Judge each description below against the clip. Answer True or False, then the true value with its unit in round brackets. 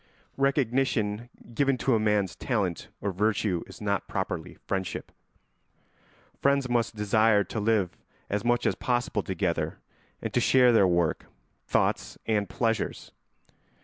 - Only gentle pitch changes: False (3.7 semitones)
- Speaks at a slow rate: True (130 wpm)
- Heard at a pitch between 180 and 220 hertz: False (110 Hz)